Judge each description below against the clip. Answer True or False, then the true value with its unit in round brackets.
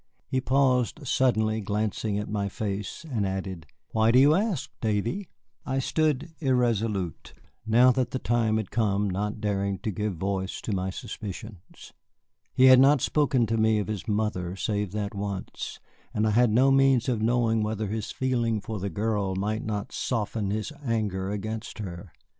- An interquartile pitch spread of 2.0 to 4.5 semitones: True (3.5 semitones)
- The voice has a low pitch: True (110 Hz)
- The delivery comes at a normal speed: True (170 wpm)